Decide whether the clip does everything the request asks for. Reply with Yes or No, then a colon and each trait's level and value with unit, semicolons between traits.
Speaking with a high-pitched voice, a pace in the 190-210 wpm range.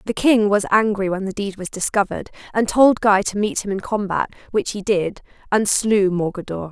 Yes: high, 200 Hz; fast, 205 wpm